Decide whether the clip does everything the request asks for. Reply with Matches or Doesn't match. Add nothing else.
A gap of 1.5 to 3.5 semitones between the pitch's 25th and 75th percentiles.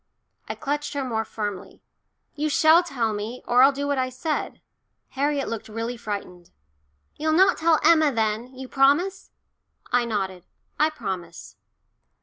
Doesn't match